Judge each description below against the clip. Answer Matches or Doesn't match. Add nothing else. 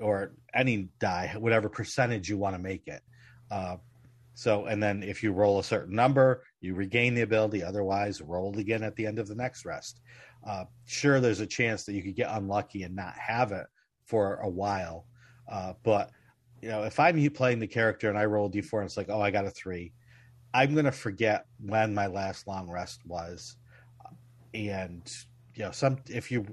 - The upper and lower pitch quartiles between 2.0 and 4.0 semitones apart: Matches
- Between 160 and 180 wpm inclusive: Doesn't match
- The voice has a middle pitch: Doesn't match